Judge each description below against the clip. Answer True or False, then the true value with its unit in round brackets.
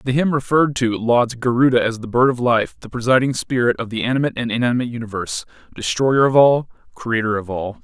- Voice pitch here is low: True (120 Hz)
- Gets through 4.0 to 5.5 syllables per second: False (6.4 syllables/s)